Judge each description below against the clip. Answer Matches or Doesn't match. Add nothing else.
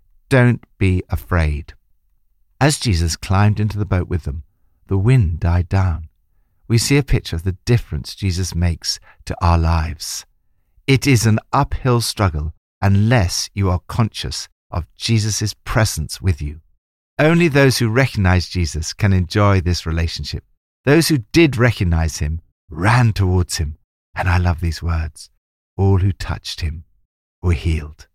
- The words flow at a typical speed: Matches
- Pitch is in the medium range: Doesn't match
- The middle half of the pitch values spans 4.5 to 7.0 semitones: Matches